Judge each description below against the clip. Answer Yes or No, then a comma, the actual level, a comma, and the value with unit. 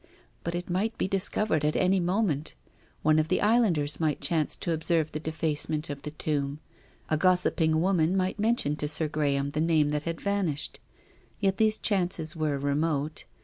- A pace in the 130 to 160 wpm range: No, average, 180 wpm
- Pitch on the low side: No, medium, 160 Hz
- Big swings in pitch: No, average, 3.6 semitones